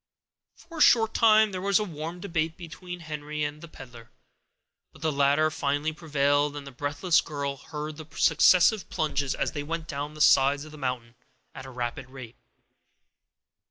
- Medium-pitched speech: Yes, medium, 150 Hz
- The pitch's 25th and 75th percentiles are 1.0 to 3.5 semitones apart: Yes, average, 2.9 semitones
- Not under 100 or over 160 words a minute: No, average, 175 wpm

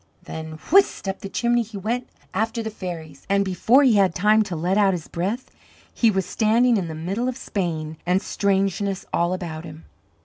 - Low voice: No, high, 195 Hz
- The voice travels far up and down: No, average, 4.1 semitones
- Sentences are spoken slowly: No, average, 195 wpm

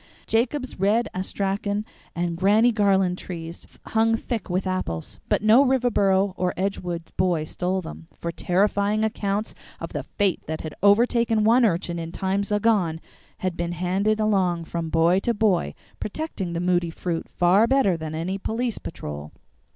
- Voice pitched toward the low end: No, high, 190 Hz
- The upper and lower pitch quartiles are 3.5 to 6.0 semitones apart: Yes, average, 3.8 semitones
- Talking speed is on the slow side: No, average, 155 wpm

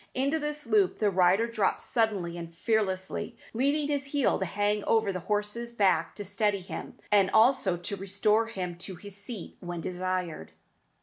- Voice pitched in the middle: No, high, 205 Hz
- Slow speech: No, average, 170 wpm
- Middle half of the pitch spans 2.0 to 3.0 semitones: No, average, 3.6 semitones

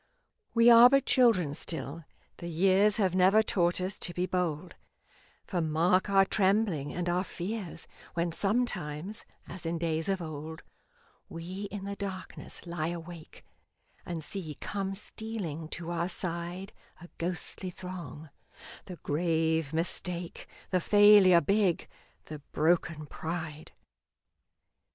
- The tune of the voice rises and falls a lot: No, average, 3.2 semitones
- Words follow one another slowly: Yes, slow, 125 wpm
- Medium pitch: Yes, medium, 175 Hz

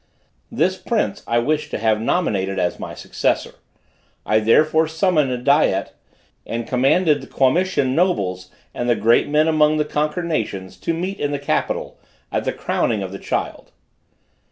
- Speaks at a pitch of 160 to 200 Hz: No, medium, 140 Hz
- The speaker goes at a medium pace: Yes, average, 160 wpm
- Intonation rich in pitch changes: Yes, wide, 6.0 semitones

